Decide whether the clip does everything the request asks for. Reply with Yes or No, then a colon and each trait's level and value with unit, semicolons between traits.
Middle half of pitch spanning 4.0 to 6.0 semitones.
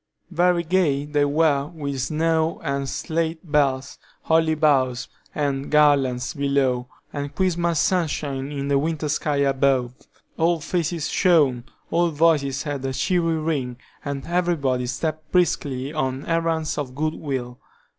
No: average, 3.1 semitones